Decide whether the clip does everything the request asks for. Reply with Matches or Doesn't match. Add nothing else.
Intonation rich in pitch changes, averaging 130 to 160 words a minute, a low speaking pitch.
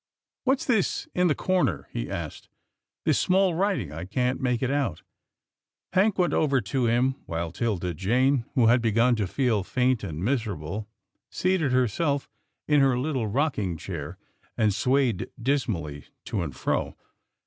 Matches